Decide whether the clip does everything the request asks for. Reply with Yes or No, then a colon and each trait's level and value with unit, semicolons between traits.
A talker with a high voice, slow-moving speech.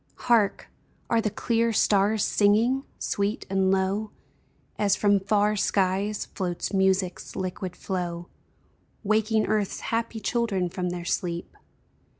Yes: high, 200 Hz; slow, 120 wpm